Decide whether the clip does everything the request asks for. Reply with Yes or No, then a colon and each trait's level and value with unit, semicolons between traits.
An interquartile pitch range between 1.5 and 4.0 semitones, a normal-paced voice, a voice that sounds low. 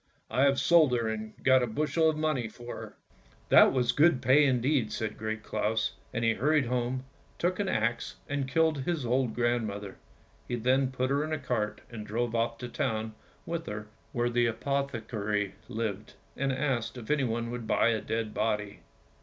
Yes: average, 3.7 semitones; average, 195 wpm; low, 120 Hz